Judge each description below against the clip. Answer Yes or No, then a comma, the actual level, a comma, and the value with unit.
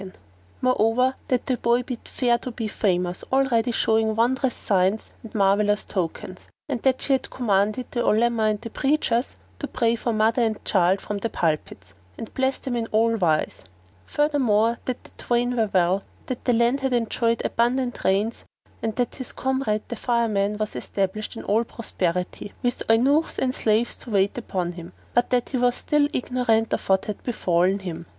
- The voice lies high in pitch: Yes, high, 225 Hz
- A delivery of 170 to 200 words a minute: Yes, average, 180 wpm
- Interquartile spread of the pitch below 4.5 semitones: Yes, average, 3.4 semitones